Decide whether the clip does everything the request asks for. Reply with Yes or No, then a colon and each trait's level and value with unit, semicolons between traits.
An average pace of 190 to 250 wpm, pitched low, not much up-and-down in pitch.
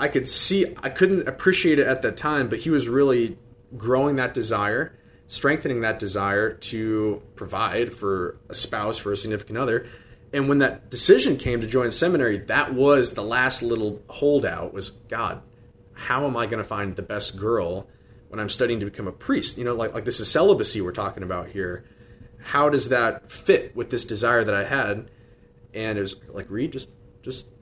No: average, 195 wpm; low, 120 Hz; average, 3.8 semitones